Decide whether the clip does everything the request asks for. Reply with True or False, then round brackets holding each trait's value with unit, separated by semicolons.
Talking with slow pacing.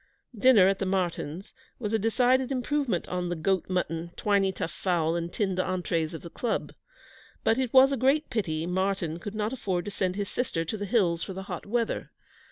False (200 wpm)